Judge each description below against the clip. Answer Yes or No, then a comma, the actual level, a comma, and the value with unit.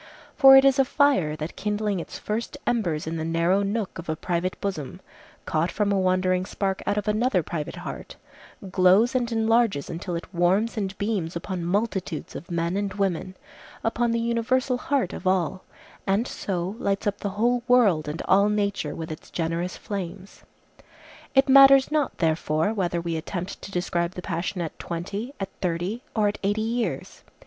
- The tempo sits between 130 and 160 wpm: No, average, 175 wpm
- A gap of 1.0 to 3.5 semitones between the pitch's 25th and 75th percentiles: No, average, 4.5 semitones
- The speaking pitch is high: Yes, high, 195 Hz